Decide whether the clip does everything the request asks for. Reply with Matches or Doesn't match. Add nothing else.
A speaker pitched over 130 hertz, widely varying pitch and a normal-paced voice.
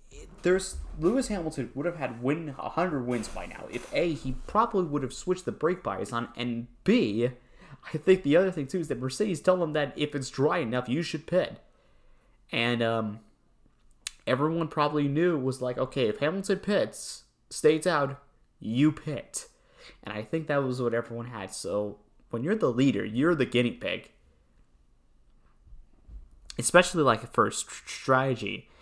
Matches